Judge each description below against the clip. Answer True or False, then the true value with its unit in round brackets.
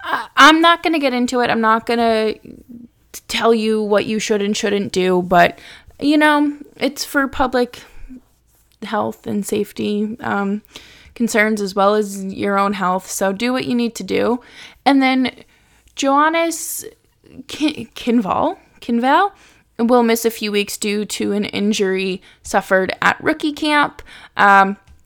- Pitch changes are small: False (4.3 semitones)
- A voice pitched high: True (230 Hz)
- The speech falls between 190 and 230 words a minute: False (150 wpm)